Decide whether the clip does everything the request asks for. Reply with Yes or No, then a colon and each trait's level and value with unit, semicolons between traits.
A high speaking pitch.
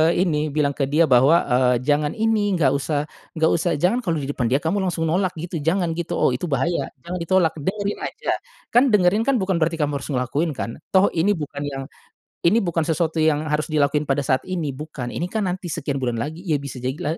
No: medium, 160 Hz